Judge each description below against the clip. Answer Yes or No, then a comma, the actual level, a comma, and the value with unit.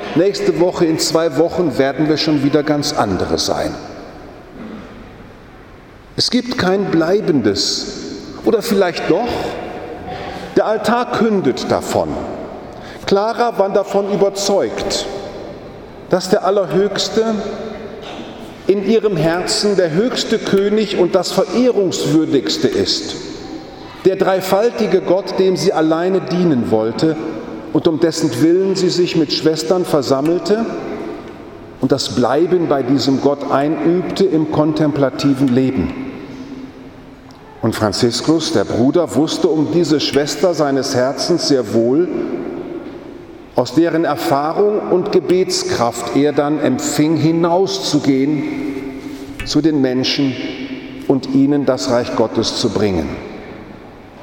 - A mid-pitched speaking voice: Yes, medium, 170 Hz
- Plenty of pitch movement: Yes, wide, 6.0 semitones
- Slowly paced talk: Yes, slow, 110 wpm